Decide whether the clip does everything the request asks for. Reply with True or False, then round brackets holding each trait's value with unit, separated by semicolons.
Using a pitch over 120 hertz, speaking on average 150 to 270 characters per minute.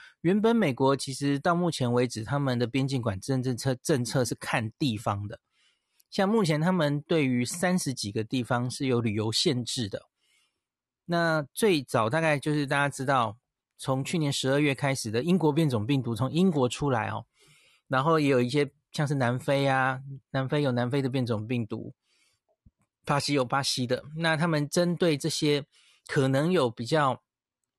True (135 Hz; 255 characters per minute)